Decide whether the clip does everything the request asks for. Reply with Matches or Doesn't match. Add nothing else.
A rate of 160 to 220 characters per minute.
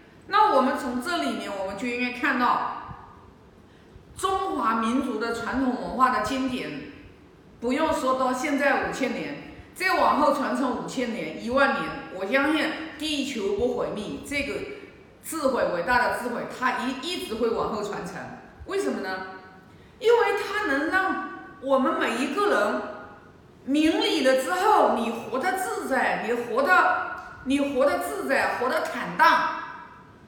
Matches